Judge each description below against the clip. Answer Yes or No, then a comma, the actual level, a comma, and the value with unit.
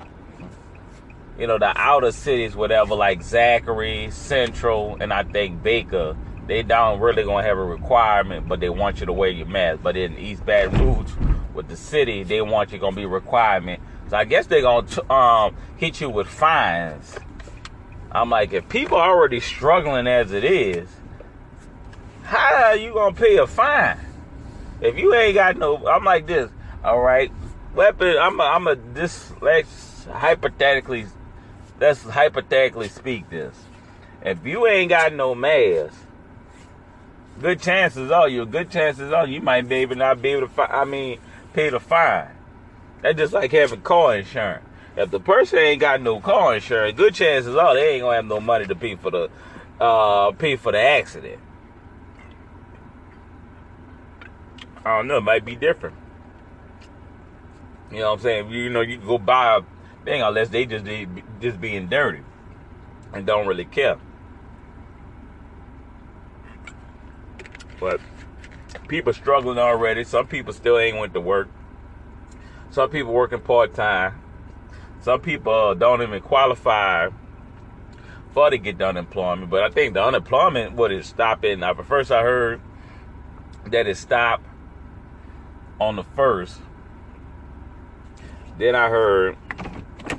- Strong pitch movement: Yes, wide, 6.5 semitones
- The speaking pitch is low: Yes, low, 105 Hz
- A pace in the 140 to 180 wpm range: Yes, average, 150 wpm